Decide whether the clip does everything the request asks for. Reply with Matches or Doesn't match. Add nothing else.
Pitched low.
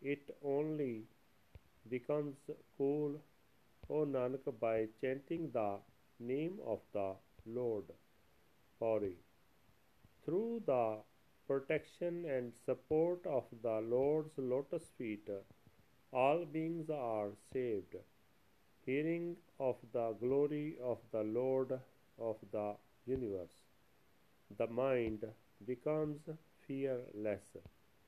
Matches